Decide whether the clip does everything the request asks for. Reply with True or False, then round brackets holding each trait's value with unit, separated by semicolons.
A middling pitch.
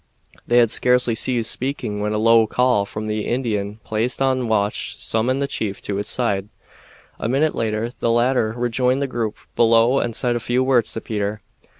False (115 Hz)